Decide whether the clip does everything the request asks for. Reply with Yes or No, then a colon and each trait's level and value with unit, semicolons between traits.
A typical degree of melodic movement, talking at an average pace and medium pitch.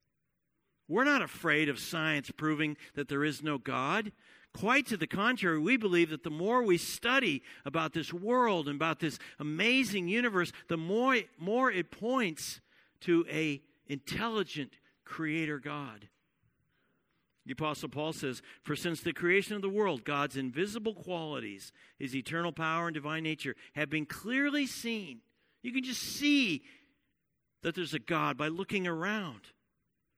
No: wide, 6.3 semitones; average, 150 wpm; medium, 170 Hz